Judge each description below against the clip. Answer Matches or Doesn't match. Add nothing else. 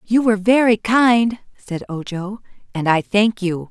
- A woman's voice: Matches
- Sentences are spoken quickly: Doesn't match